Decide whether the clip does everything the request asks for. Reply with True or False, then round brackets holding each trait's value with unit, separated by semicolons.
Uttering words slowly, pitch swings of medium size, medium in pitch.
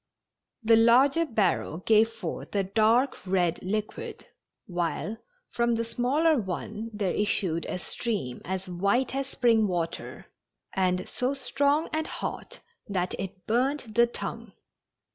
False (130 wpm; 4.8 semitones; 220 Hz)